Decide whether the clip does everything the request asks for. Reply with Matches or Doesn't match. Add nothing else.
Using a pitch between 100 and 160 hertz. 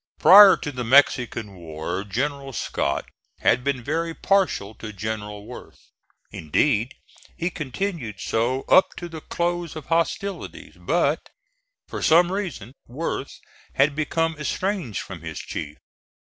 Matches